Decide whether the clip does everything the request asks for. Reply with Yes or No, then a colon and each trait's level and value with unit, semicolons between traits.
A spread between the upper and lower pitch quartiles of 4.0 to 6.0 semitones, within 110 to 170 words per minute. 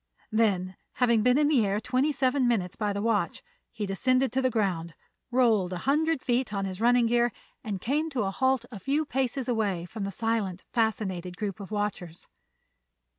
No: average, 4.5 semitones; average, 185 wpm